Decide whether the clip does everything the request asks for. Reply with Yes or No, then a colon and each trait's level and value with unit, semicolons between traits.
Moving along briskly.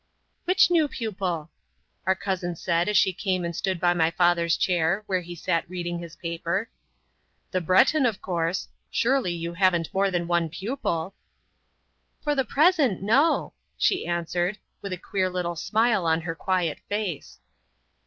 No: average, 155 wpm